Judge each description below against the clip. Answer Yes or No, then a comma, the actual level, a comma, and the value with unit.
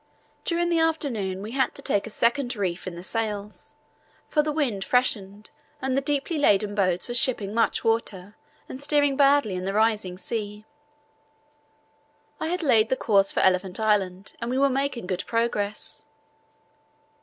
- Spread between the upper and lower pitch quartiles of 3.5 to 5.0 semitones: No, wide, 5.4 semitones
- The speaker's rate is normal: Yes, average, 165 wpm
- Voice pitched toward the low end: No, high, 225 Hz